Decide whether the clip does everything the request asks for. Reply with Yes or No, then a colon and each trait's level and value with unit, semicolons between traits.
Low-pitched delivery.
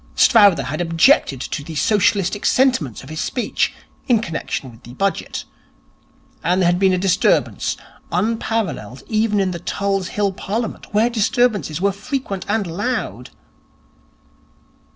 No: high, 195 Hz